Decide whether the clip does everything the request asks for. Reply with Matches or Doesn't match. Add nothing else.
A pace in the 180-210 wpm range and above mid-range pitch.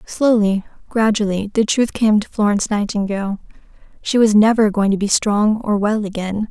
Doesn't match